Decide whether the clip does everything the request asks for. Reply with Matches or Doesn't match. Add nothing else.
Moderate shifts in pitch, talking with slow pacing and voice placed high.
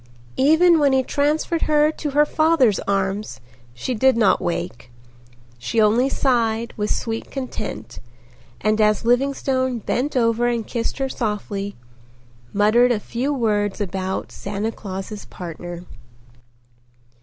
Matches